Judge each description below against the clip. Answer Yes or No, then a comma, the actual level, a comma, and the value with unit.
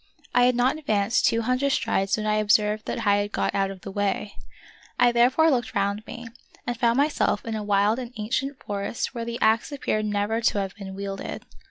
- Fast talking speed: Yes, fast, 210 wpm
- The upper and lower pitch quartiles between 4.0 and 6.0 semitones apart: No, average, 3.1 semitones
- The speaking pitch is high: Yes, high, 220 Hz